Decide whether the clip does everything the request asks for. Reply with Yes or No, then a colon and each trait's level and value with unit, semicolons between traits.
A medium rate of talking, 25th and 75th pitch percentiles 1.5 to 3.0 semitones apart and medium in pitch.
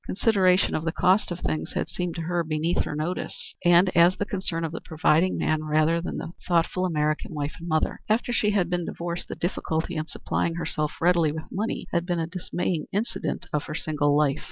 No: fast, 210 wpm; narrow, 2.6 semitones; medium, 170 Hz